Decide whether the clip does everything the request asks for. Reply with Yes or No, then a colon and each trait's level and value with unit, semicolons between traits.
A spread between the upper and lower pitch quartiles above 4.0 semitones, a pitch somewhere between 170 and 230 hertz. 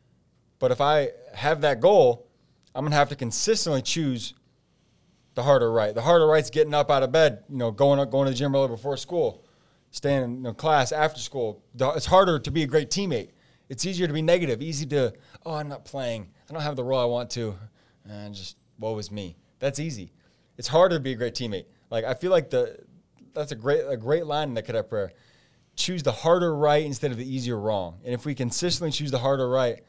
No: average, 4.7 semitones; medium, 140 Hz